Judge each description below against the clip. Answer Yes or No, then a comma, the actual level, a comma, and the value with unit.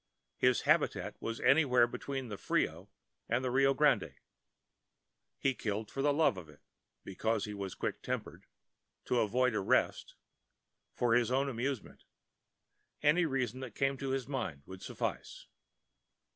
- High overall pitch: No, low, 125 Hz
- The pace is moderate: No, slow, 130 wpm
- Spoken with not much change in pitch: No, average, 3.9 semitones